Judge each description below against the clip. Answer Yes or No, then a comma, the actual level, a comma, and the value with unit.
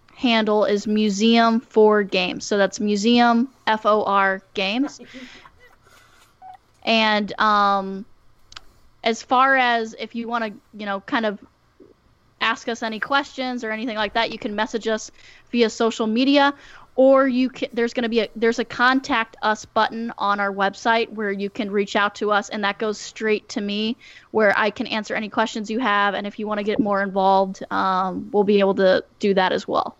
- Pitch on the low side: No, high, 220 Hz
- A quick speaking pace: No, average, 180 wpm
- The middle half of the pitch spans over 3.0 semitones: No, narrow, 2.5 semitones